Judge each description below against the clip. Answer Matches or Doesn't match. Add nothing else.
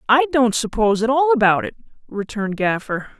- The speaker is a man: Doesn't match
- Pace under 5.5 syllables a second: Doesn't match